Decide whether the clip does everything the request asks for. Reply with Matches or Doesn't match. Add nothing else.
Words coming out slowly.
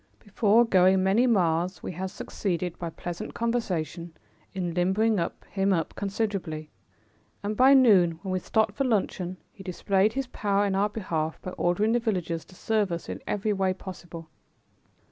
Doesn't match